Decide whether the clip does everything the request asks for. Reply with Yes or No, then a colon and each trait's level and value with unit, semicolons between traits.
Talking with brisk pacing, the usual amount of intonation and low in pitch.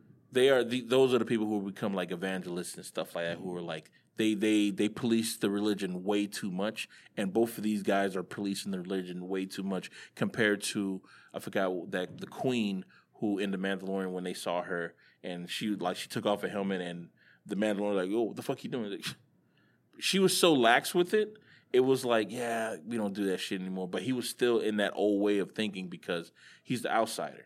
Yes: fast, 225 wpm; average, 3.0 semitones; low, 100 Hz